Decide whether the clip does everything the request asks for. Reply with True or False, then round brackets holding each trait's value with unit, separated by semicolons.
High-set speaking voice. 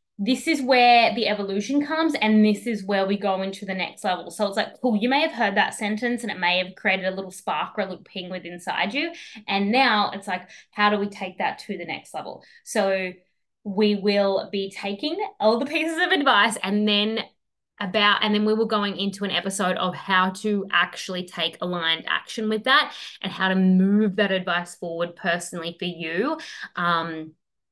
True (200 Hz)